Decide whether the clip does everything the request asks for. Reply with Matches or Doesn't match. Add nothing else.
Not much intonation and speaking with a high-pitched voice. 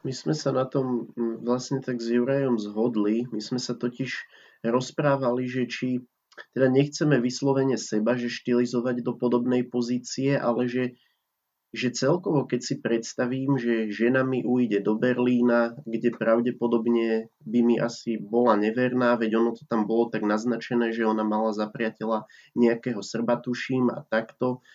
Doesn't match